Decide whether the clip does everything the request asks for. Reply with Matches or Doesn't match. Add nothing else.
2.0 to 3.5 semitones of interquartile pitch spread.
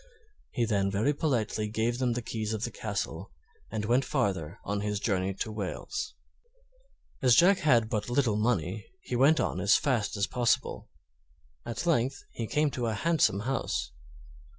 Doesn't match